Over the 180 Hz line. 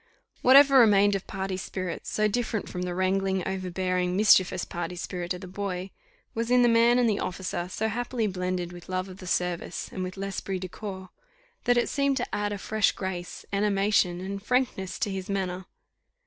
Yes: high, 190 Hz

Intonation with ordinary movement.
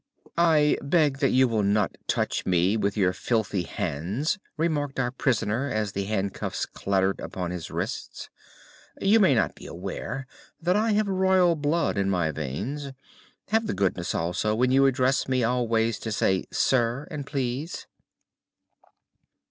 No: wide, 6.7 semitones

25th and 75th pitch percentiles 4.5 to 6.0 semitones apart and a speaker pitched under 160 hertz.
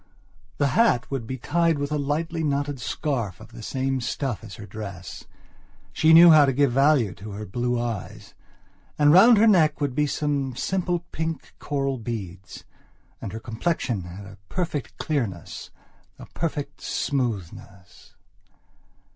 Yes: wide, 5.5 semitones; low, 135 Hz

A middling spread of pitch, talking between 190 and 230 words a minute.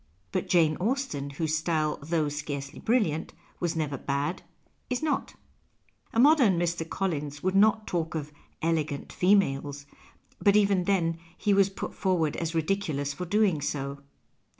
No: average, 4.9 semitones; average, 155 wpm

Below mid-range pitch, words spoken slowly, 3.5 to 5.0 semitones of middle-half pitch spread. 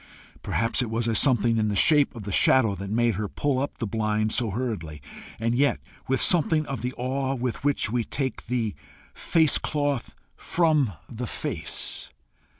No: low, 120 Hz; average, 170 wpm; average, 4.0 semitones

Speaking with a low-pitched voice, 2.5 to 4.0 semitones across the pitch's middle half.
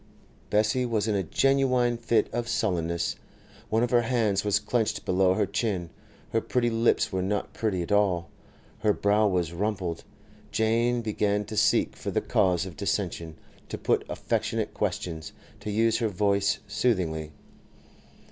Yes: low, 105 Hz; average, 3.7 semitones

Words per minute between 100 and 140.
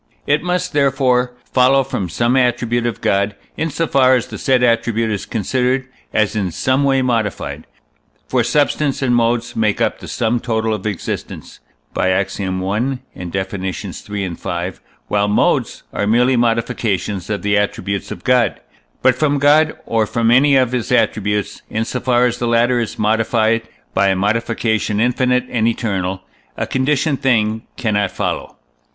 No: average, 165 wpm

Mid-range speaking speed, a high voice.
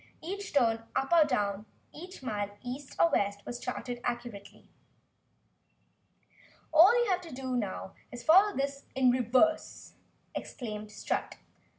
No: slow, 125 wpm; very high, 255 Hz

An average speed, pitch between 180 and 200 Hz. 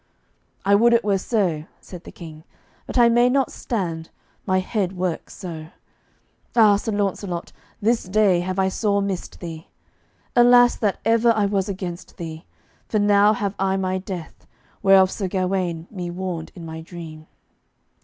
Yes: average, 160 wpm; high, 190 Hz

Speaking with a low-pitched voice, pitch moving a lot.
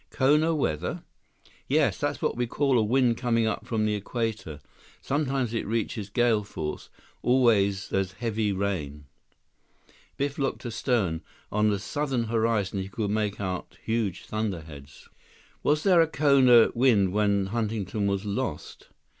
No: low, 110 Hz; average, 3.7 semitones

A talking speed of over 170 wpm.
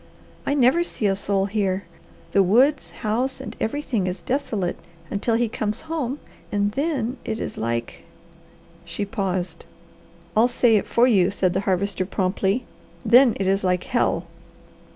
No: average, 155 wpm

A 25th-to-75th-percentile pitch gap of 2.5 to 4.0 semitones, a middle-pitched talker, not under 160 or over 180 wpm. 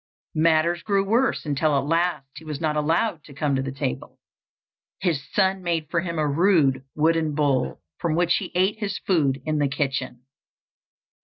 Yes: average, 3.6 semitones; medium, 155 Hz; average, 175 wpm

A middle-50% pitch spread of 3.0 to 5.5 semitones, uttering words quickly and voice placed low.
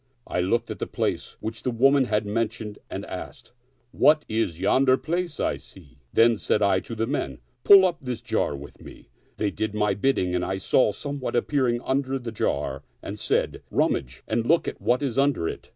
Yes: average, 5.1 semitones; fast, 215 wpm; low, 115 Hz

